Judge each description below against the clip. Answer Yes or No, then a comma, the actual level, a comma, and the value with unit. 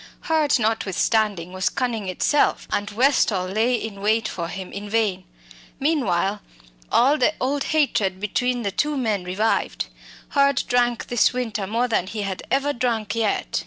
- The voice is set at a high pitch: Yes, high, 225 Hz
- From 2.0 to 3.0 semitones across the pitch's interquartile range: No, average, 4.1 semitones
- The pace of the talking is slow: No, average, 155 wpm